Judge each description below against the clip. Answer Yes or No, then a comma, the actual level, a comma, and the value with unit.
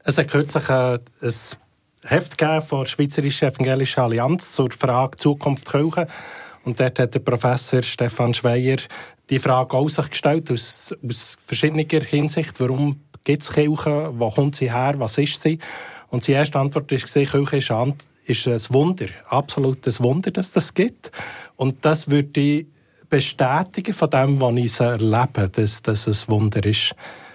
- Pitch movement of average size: Yes, average, 3.3 semitones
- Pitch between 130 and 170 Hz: Yes, low, 135 Hz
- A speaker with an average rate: Yes, average, 145 wpm